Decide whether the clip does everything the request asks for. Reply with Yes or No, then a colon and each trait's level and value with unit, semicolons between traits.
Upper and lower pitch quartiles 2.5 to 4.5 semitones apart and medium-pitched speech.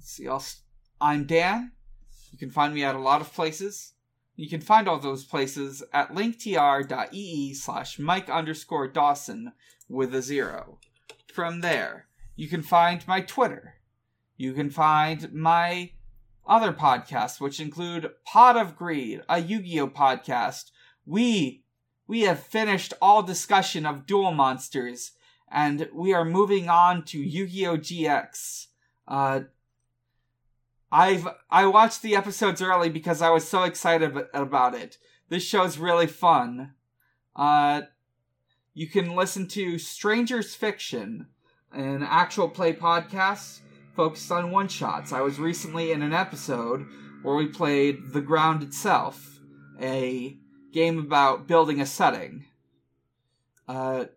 No: average, 5.2 semitones; medium, 155 Hz